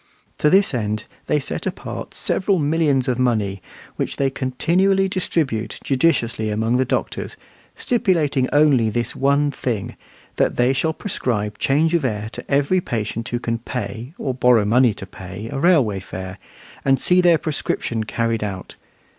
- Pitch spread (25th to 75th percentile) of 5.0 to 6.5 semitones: Yes, wide, 5.4 semitones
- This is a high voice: No, low, 130 Hz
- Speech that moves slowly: No, average, 155 wpm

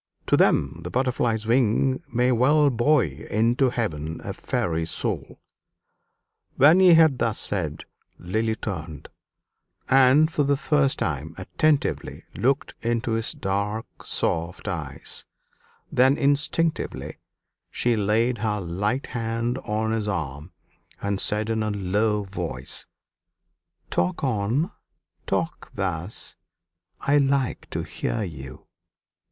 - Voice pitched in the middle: No, low, 110 Hz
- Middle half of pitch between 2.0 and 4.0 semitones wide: No, average, 5.3 semitones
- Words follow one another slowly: Yes, slow, 115 wpm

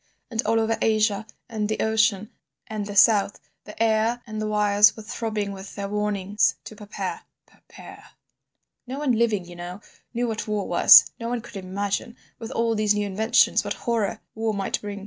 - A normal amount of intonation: No, narrow, 1.8 semitones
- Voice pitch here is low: No, high, 215 Hz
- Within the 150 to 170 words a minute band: No, average, 180 wpm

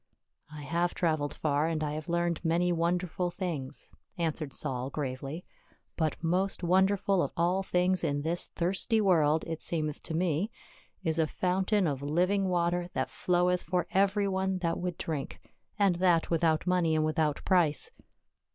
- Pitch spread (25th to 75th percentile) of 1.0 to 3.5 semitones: Yes, average, 2.7 semitones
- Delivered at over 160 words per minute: Yes, average, 170 wpm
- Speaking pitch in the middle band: Yes, medium, 170 Hz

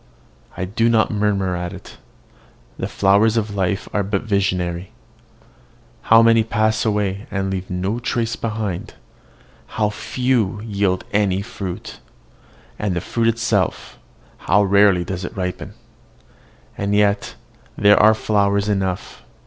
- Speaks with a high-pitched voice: No, low, 100 Hz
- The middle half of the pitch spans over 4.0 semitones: No, narrow, 2.4 semitones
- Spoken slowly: Yes, slow, 130 wpm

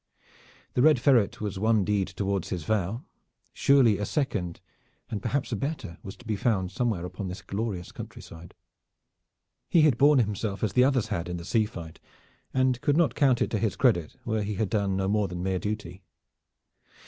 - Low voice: Yes, low, 105 Hz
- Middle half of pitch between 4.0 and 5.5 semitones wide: Yes, average, 4.5 semitones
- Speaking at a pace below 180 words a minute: No, average, 190 wpm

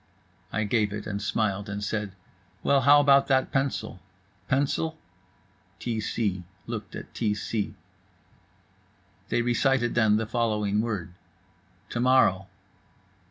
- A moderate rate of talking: No, slow, 115 wpm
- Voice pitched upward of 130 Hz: No, low, 110 Hz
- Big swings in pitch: No, average, 3.8 semitones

